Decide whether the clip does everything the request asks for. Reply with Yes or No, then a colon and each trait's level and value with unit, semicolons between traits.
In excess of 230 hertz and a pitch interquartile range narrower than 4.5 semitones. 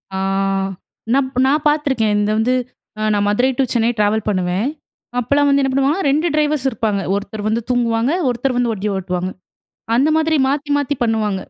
No: high, 240 Hz; average, 4.8 semitones